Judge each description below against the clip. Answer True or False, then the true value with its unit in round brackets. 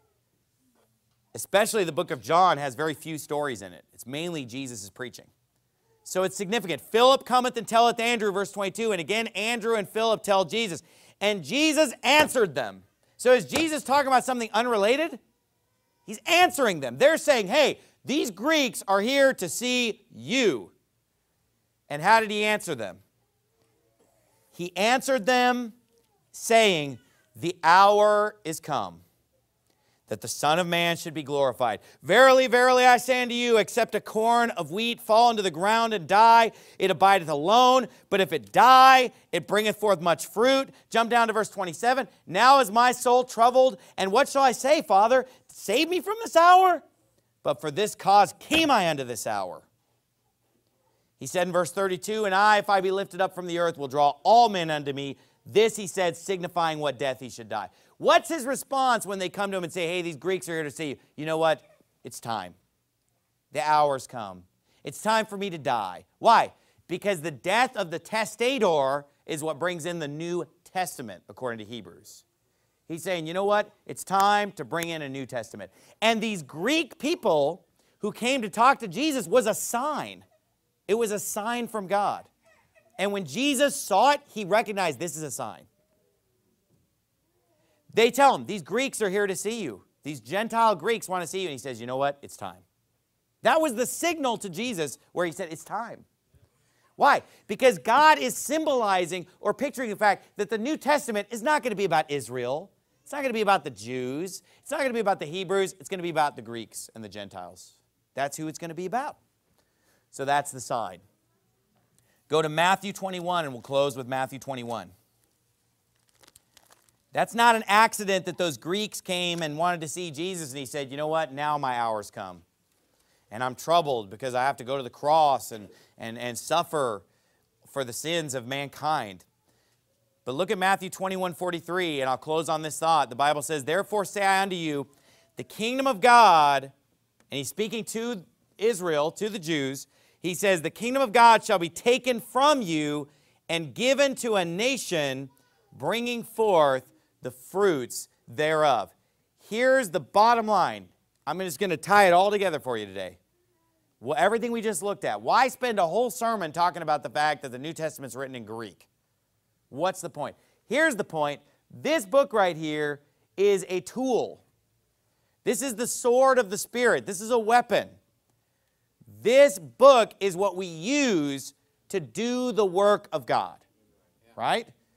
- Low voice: False (190 Hz)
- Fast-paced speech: False (185 wpm)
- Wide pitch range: True (7.8 semitones)